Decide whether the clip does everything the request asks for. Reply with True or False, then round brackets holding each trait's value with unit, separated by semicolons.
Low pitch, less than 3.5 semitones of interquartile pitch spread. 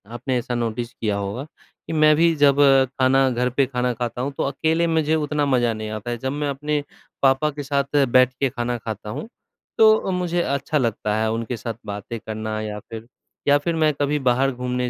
False (130 Hz; 4.0 semitones)